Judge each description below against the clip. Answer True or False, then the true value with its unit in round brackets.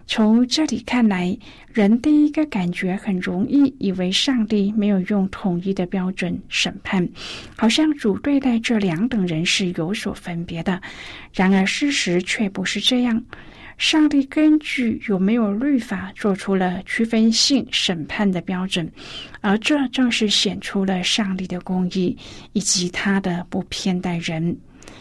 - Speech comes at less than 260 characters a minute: True (220 characters per minute)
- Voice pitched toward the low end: False (205 Hz)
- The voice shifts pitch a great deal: False (4.2 semitones)